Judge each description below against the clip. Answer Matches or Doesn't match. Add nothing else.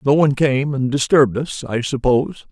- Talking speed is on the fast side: Doesn't match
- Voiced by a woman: Doesn't match